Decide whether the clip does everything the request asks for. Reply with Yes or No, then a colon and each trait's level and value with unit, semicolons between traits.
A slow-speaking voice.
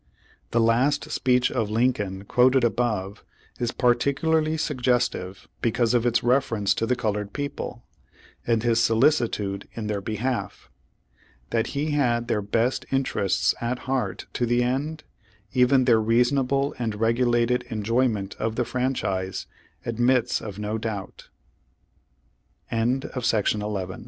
Yes: slow, 120 wpm